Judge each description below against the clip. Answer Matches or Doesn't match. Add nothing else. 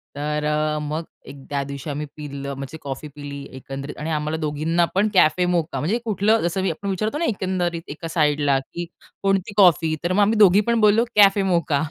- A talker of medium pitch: Matches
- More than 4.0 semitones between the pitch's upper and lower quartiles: Matches